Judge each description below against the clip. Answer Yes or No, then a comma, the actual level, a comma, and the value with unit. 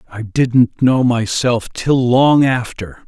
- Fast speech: No, slow, 135 wpm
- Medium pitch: No, low, 120 Hz